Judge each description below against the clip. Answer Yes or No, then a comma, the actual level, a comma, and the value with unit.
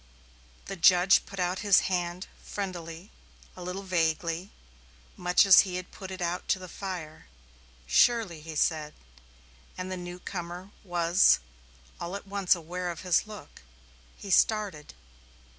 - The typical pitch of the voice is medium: Yes, medium, 180 Hz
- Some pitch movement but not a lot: No, narrow, 2.0 semitones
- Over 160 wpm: No, average, 140 wpm